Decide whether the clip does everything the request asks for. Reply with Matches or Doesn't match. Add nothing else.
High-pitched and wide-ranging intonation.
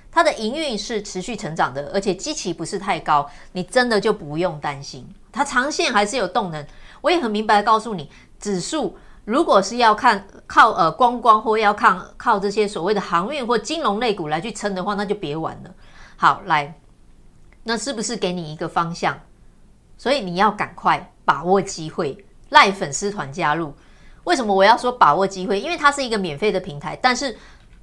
Doesn't match